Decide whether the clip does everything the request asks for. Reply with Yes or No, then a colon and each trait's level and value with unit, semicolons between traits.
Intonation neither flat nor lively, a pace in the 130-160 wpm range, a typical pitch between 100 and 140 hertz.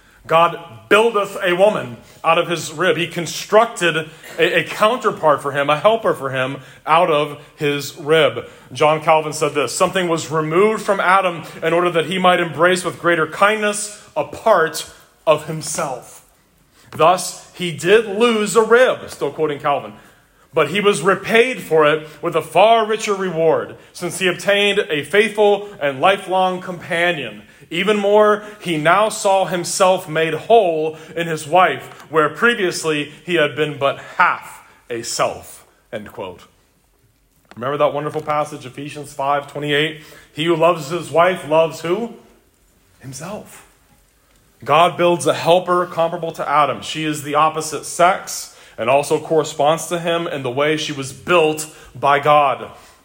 No: average, 3.5 semitones; average, 155 wpm; medium, 165 Hz